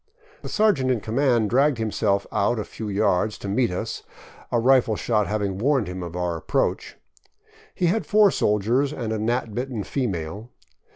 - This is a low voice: Yes, low, 110 Hz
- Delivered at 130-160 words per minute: No, average, 170 wpm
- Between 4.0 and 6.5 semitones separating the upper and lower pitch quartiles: Yes, average, 4.4 semitones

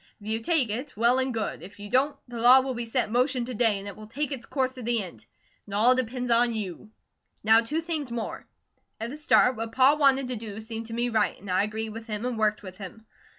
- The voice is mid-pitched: No, high, 230 Hz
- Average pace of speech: No, fast, 260 wpm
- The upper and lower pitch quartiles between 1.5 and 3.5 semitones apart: Yes, average, 3.0 semitones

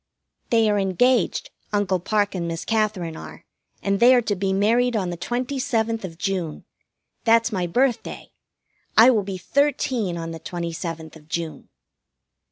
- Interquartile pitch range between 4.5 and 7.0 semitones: Yes, average, 4.9 semitones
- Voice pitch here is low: No, high, 200 Hz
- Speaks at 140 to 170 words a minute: Yes, average, 165 wpm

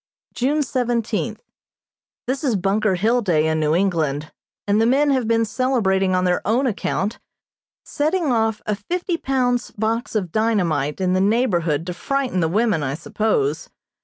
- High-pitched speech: Yes, high, 220 Hz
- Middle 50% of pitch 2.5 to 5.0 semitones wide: No, wide, 5.4 semitones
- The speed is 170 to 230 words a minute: No, average, 160 wpm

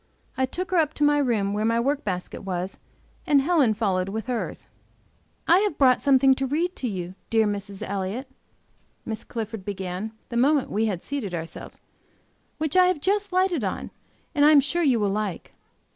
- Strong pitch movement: Yes, wide, 6.5 semitones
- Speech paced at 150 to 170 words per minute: No, average, 190 wpm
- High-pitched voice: Yes, high, 240 Hz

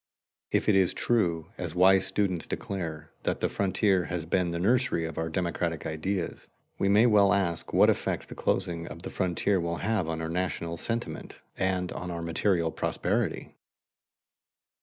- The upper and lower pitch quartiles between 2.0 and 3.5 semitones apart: Yes, average, 2.7 semitones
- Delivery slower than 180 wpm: Yes, average, 165 wpm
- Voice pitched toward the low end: Yes, very low, 90 Hz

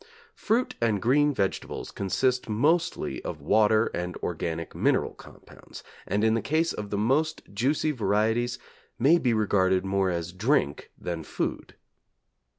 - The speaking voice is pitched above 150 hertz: No, low, 110 Hz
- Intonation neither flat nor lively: No, wide, 5.8 semitones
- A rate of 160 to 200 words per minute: No, average, 140 wpm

